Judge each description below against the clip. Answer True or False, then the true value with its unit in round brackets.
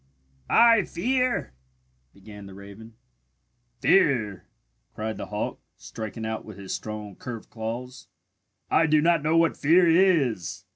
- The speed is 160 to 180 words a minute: False (135 wpm)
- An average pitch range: False (8.1 semitones)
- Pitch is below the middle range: True (115 Hz)